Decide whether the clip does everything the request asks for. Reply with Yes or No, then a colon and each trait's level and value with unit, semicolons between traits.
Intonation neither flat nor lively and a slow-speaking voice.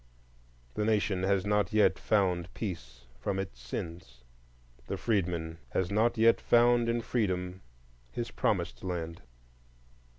Yes: average, 4.1 semitones; slow, 125 wpm